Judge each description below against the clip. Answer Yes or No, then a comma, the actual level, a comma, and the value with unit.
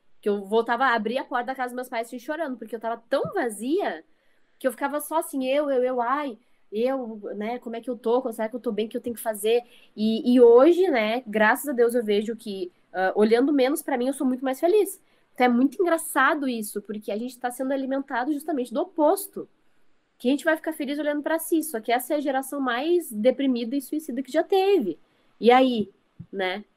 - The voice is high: Yes, very high, 255 Hz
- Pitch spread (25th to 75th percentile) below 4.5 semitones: Yes, average, 4.1 semitones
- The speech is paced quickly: Yes, fast, 235 wpm